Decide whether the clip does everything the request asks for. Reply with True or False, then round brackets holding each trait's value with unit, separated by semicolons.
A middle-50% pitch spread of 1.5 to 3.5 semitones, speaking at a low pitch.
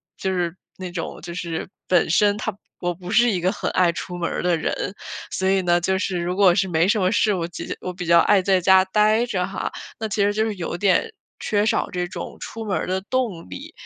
False (2.6 semitones; 185 Hz)